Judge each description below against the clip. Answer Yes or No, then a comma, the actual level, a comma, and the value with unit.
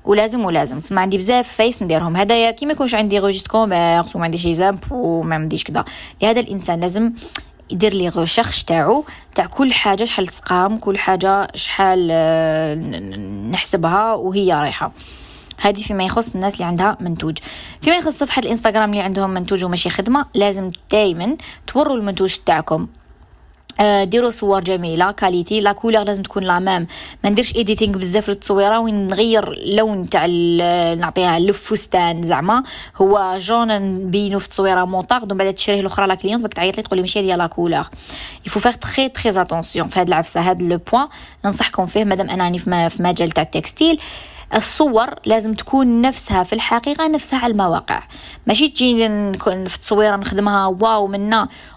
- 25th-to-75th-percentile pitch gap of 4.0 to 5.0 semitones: No, average, 3.5 semitones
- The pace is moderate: No, fast, 155 wpm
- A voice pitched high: Yes, high, 200 Hz